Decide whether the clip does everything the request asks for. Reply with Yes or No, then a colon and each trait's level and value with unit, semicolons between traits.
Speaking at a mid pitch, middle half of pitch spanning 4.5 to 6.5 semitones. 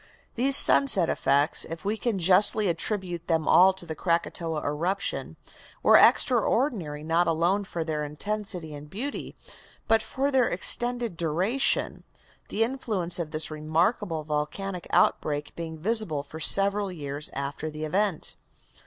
Yes: medium, 175 Hz; average, 5.2 semitones